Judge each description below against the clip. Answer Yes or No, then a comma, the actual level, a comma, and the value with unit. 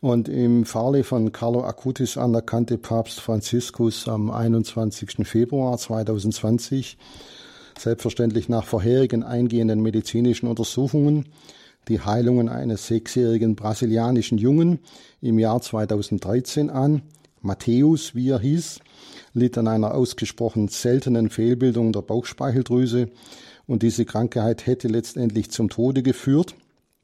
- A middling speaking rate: No, slow, 110 wpm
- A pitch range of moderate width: No, narrow, 1.9 semitones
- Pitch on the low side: Yes, low, 120 Hz